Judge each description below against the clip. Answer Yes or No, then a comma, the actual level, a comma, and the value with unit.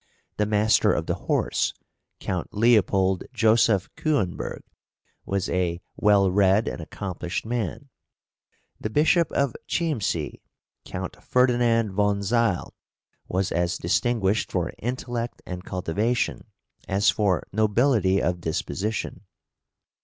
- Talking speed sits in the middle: No, slow, 110 wpm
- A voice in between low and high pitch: No, low, 105 Hz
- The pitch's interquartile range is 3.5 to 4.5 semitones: Yes, average, 3.9 semitones